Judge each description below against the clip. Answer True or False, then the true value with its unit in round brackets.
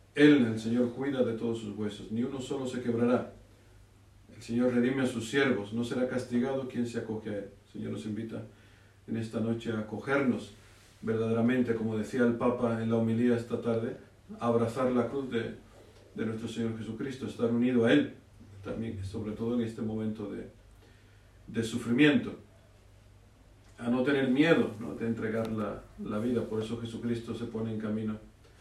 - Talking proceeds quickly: False (180 wpm)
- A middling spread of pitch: False (2.1 semitones)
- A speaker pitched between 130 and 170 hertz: False (115 Hz)